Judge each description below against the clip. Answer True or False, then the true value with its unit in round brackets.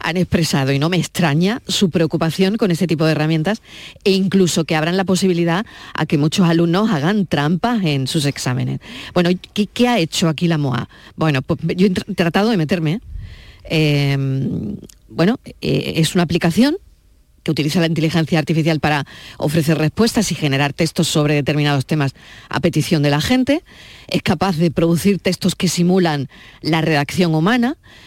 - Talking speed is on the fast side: False (170 wpm)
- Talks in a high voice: False (170 Hz)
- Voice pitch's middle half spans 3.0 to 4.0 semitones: True (3.6 semitones)